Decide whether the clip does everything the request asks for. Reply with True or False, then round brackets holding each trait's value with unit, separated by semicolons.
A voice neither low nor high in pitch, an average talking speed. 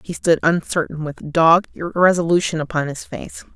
True (165 Hz; 150 wpm)